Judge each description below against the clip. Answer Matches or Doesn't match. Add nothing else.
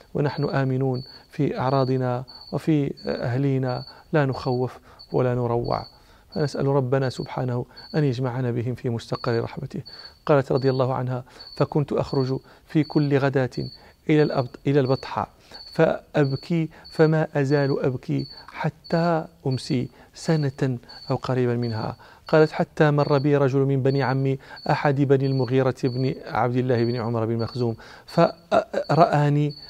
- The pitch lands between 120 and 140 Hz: Matches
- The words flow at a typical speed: Matches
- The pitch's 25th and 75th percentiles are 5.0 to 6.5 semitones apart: Doesn't match